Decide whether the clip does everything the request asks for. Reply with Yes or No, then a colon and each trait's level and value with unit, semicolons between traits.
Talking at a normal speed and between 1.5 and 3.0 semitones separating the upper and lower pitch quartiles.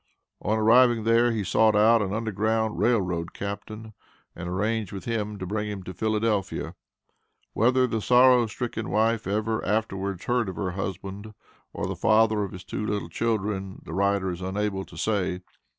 Yes: average, 170 wpm; narrow, 2.6 semitones